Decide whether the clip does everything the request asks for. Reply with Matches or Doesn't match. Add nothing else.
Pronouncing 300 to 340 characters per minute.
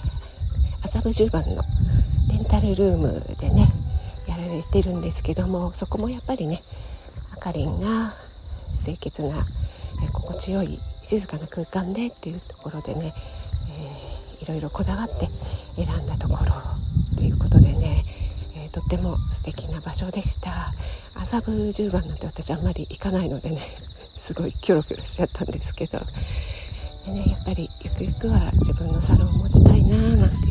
Matches